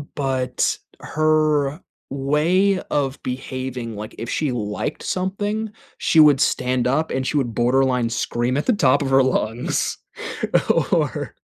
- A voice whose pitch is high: No, low, 135 Hz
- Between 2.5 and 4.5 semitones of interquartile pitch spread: Yes, average, 3.6 semitones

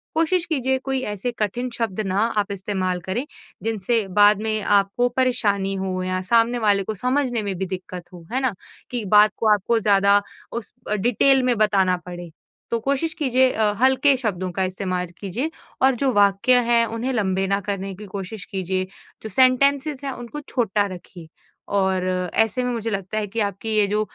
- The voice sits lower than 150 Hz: No, high, 215 Hz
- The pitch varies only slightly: No, average, 4.3 semitones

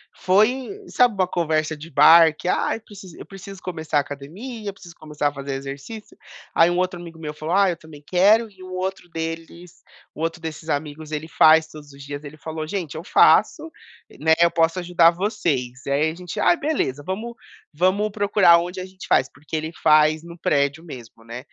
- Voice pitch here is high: No, medium, 165 Hz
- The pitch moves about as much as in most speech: Yes, average, 3.6 semitones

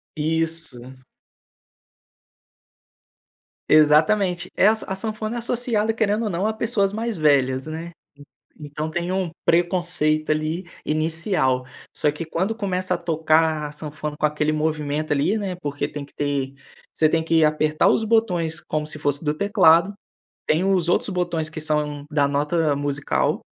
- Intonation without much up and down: No, average, 3.7 semitones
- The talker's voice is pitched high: No, medium, 160 Hz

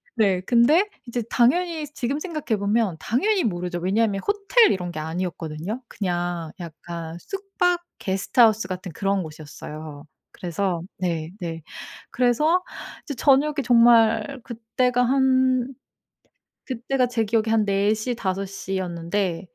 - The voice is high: Yes, high, 215 Hz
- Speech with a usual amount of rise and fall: No, wide, 6.3 semitones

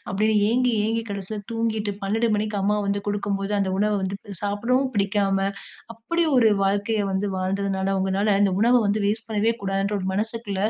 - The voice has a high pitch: Yes, high, 205 Hz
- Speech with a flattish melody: Yes, narrow, 2.1 semitones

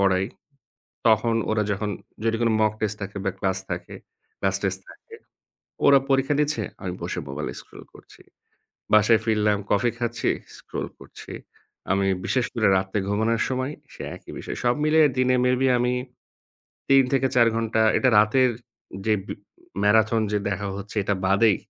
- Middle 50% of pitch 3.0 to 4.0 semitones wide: Yes, average, 3.6 semitones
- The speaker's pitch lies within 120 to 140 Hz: No, low, 110 Hz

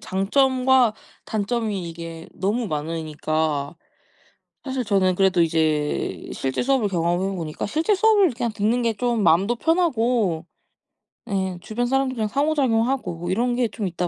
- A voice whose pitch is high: Yes, high, 210 Hz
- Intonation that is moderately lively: No, wide, 6.5 semitones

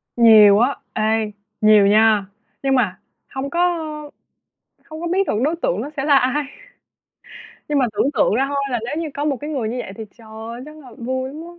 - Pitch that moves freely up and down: No, average, 4.7 semitones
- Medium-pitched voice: No, very high, 255 Hz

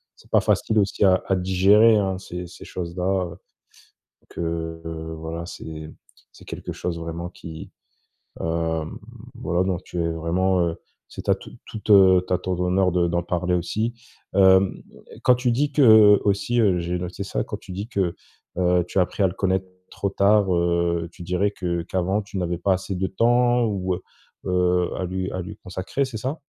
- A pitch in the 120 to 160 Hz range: No, very low, 90 Hz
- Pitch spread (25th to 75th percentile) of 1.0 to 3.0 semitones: Yes, narrow, 2.5 semitones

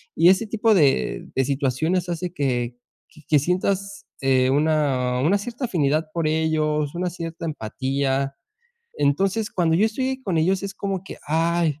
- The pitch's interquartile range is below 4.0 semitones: No, average, 4.9 semitones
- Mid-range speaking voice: Yes, medium, 160 Hz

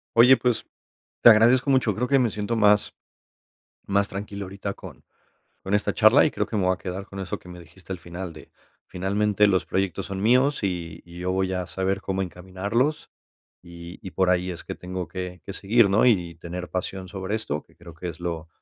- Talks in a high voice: No, very low, 95 Hz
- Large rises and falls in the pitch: No, average, 2.8 semitones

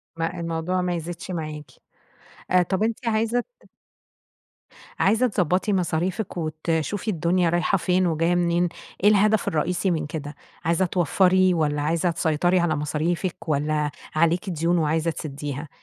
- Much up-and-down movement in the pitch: No, average, 2.8 semitones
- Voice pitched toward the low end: No, medium, 170 Hz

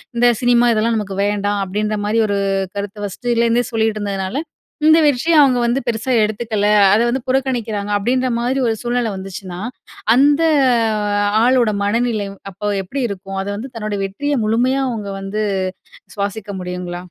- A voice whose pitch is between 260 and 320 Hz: No, high, 220 Hz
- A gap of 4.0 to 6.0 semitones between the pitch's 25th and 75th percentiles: No, average, 3.3 semitones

